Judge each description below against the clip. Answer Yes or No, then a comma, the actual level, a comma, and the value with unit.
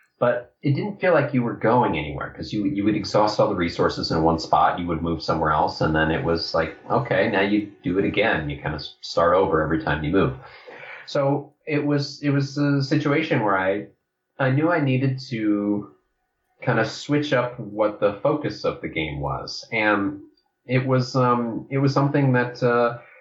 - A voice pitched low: Yes, low, 125 Hz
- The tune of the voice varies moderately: No, wide, 5.8 semitones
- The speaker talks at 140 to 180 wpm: No, fast, 205 wpm